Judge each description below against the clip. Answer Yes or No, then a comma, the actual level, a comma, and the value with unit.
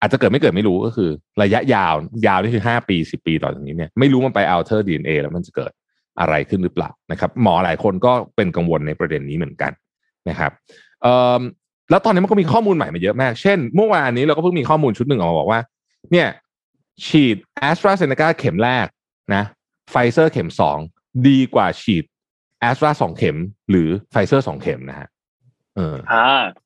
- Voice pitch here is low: Yes, low, 125 Hz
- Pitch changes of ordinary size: No, wide, 8.2 semitones